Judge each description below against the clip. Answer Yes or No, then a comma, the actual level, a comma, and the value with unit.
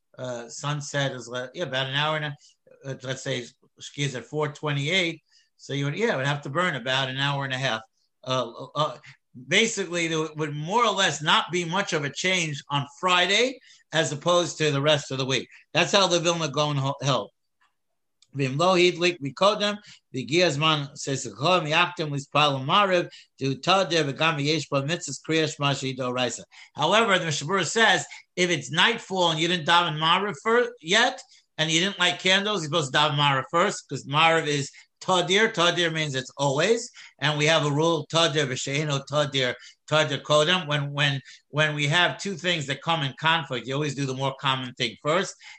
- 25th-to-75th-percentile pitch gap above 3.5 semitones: Yes, average, 4.0 semitones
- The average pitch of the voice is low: No, medium, 155 Hz